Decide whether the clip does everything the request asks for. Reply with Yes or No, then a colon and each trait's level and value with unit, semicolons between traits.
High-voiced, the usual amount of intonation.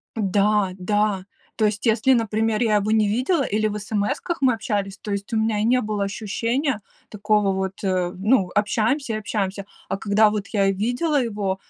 No: high, 210 Hz; narrow, 2.1 semitones